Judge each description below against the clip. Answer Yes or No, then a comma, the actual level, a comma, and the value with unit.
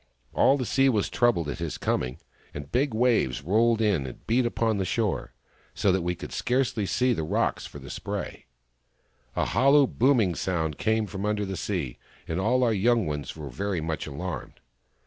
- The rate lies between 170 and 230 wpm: Yes, average, 185 wpm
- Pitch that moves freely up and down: Yes, wide, 6.3 semitones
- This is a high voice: No, low, 100 Hz